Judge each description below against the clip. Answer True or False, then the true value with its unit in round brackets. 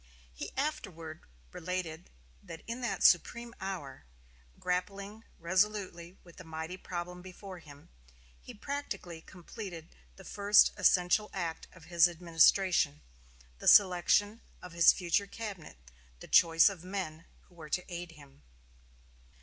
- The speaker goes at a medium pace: False (130 wpm)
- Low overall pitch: False (180 Hz)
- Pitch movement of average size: True (3.1 semitones)